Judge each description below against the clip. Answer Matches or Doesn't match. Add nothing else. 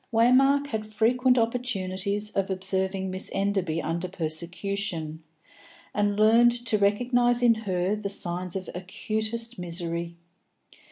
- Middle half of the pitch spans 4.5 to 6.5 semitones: Doesn't match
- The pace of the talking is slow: Matches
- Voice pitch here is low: Doesn't match